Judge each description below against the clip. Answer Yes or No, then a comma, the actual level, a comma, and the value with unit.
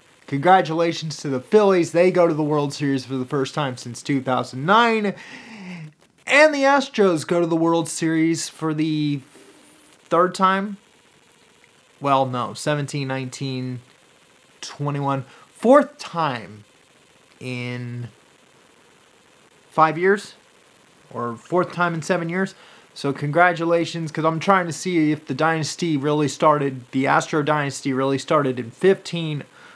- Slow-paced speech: Yes, slow, 125 wpm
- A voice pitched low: No, medium, 155 Hz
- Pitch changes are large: No, average, 4.7 semitones